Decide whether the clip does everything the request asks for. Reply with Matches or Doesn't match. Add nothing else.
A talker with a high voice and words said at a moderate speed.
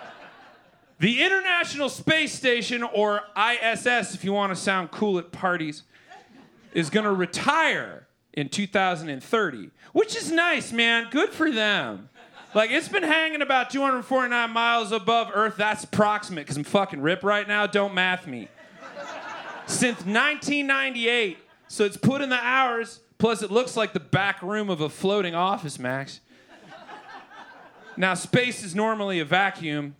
Matches